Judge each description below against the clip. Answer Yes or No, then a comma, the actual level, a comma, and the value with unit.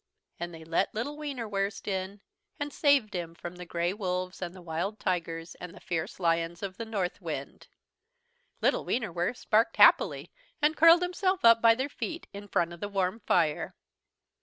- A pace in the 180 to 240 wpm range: No, average, 170 wpm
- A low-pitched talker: No, high, 195 Hz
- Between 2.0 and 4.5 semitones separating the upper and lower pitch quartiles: No, average, 5.1 semitones